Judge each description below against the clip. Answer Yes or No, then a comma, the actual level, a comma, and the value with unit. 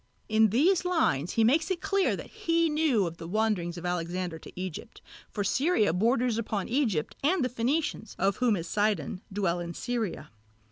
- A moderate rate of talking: Yes, average, 180 wpm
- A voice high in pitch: Yes, high, 220 Hz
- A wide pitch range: Yes, wide, 8.0 semitones